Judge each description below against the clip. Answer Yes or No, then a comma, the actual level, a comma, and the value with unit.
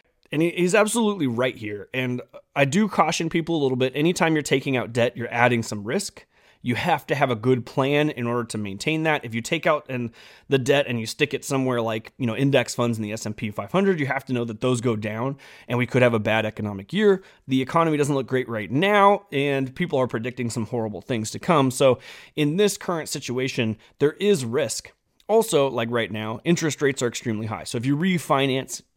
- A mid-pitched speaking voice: No, low, 130 Hz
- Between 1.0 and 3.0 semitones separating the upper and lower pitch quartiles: No, average, 4.7 semitones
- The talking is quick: Yes, fast, 225 wpm